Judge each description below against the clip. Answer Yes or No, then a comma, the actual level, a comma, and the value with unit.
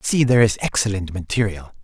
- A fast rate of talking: No, average, 195 wpm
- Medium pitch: No, low, 105 Hz